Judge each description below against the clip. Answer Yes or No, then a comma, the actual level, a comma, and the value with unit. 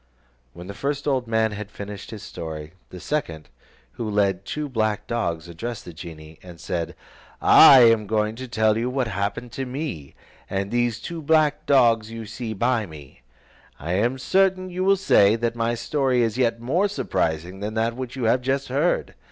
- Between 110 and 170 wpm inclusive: No, average, 195 wpm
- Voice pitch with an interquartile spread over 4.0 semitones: Yes, average, 4.7 semitones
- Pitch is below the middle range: Yes, low, 115 Hz